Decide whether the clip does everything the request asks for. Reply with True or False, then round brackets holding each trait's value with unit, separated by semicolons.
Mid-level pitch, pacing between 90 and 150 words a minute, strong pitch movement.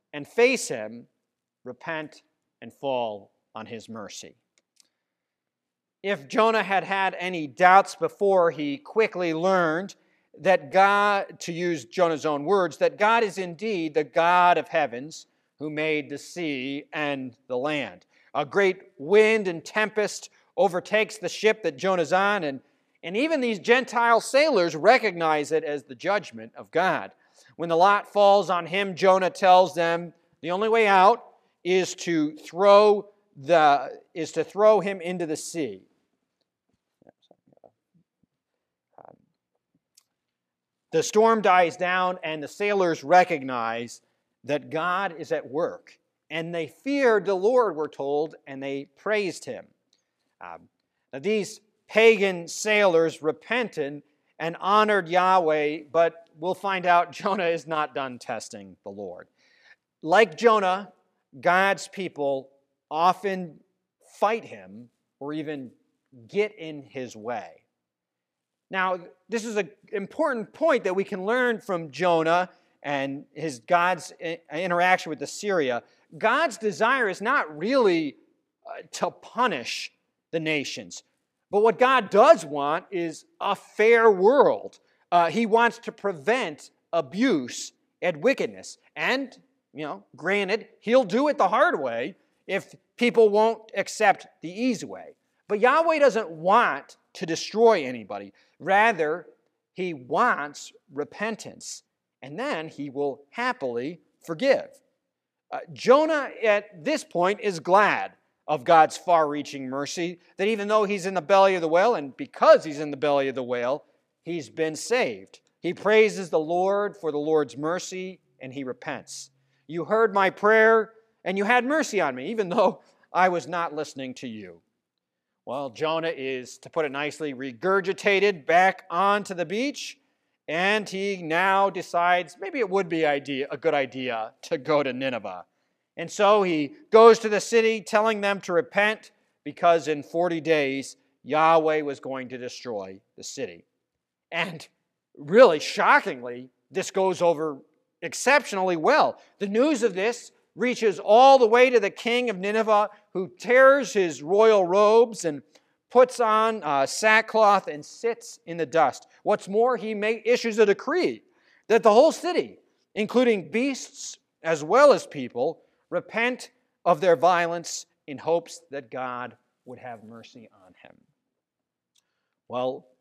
True (180 Hz; 140 wpm; 5.8 semitones)